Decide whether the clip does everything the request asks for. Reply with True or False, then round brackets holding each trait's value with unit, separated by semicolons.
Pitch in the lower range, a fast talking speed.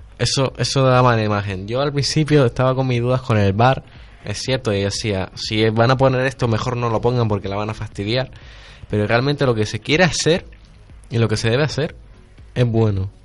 True (120 Hz; 220 wpm)